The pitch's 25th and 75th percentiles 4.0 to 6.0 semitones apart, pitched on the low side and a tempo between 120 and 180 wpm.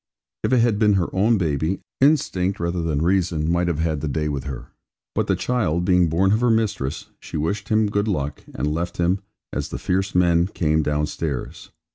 No: average, 4.4 semitones; very low, 85 Hz; average, 200 wpm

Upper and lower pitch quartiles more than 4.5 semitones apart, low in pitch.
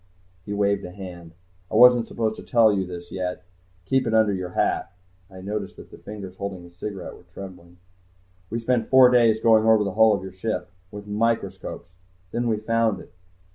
No: average, 3.3 semitones; low, 105 Hz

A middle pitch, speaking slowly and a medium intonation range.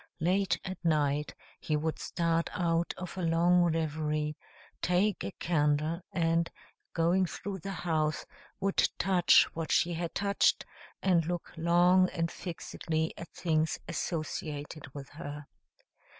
No: medium, 165 Hz; slow, 130 wpm; narrow, 2.3 semitones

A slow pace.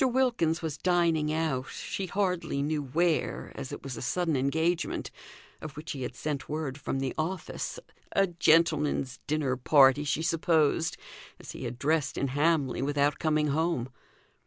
No: average, 160 wpm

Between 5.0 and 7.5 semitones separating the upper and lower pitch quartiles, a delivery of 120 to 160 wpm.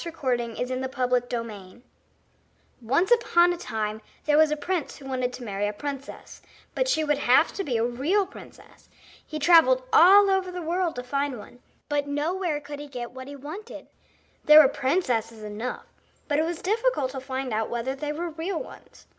No: wide, 5.5 semitones; average, 190 wpm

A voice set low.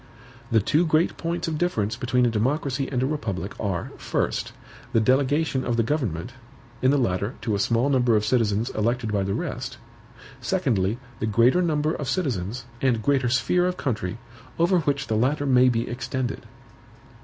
Yes: low, 125 Hz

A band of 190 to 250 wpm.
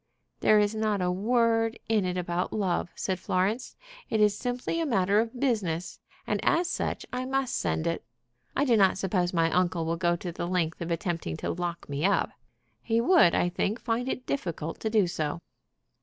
Yes: average, 195 wpm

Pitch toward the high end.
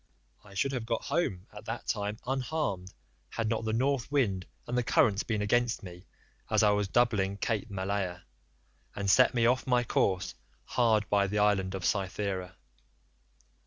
No: low, 105 Hz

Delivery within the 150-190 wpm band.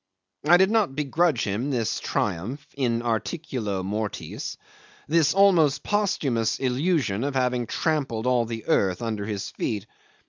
No: slow, 135 wpm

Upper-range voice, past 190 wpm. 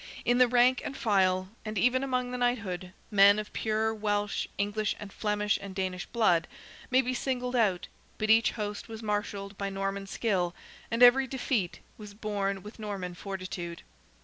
No: high, 210 Hz; average, 170 wpm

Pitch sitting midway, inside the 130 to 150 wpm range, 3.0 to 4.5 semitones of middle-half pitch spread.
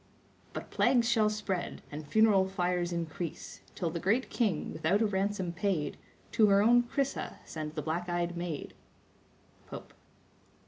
Yes: medium, 180 Hz; average, 145 wpm; average, 3.8 semitones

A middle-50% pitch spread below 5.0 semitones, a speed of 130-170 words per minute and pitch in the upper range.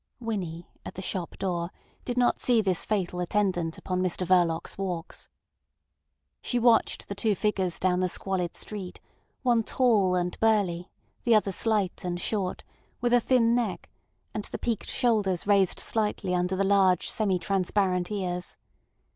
Yes: average, 3.3 semitones; average, 155 wpm; high, 195 Hz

